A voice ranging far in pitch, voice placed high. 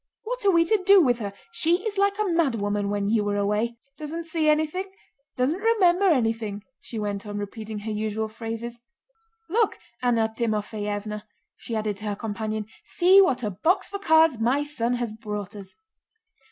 Yes: wide, 8.0 semitones; high, 235 Hz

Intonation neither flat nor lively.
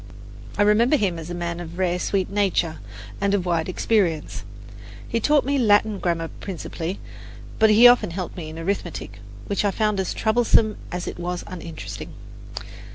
Yes: average, 3.7 semitones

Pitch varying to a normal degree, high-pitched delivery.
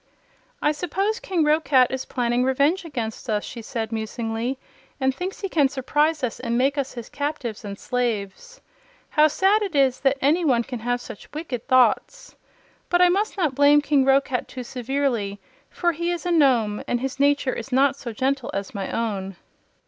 Yes: average, 4.2 semitones; very high, 270 Hz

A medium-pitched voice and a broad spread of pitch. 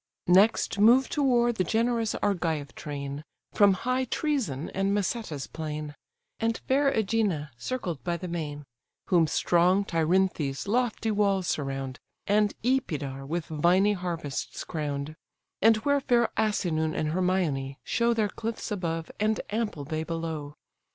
Yes: medium, 180 Hz; wide, 6.3 semitones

